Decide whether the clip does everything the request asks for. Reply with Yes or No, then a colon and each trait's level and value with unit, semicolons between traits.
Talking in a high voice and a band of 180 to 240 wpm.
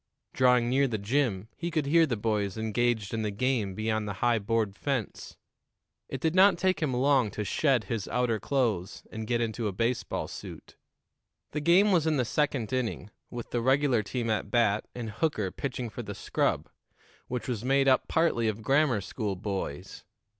No: low, 120 Hz; average, 185 wpm